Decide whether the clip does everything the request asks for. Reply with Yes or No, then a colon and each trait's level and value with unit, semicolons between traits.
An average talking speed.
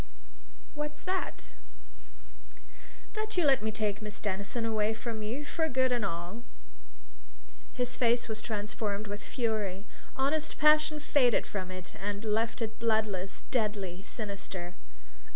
No: slow, 130 wpm